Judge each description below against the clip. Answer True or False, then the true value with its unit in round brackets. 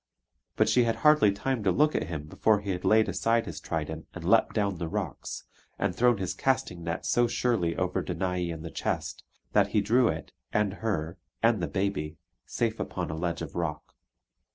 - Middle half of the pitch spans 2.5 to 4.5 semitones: False (5.1 semitones)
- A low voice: True (95 Hz)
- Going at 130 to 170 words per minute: False (200 wpm)